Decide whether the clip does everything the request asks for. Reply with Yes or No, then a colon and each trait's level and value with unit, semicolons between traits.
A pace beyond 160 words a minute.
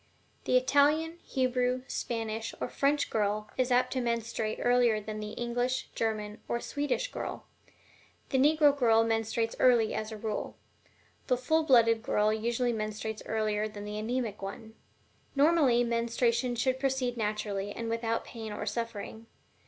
No: average, 145 wpm